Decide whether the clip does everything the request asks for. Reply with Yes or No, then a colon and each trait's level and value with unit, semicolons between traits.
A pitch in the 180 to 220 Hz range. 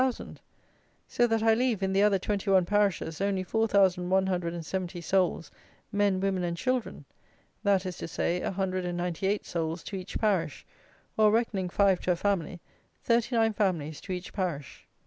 Yes: high, 190 Hz